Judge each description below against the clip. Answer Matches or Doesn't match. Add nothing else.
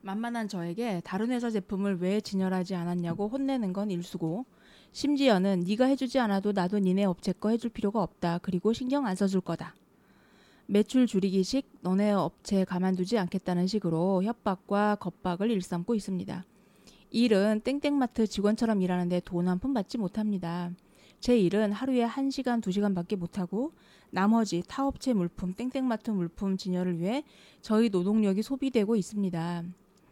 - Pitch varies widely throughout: Doesn't match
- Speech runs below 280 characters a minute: Doesn't match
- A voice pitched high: Matches